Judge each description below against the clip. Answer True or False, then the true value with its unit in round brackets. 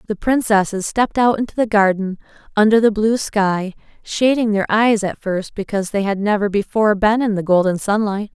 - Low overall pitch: False (210 Hz)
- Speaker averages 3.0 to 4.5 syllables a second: False (5.4 syllables/s)